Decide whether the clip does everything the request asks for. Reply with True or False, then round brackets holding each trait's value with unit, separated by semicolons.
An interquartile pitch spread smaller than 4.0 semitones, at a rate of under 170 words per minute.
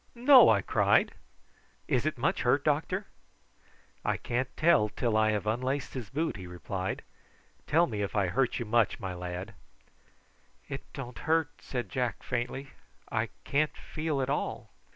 False (5.2 semitones; 155 wpm)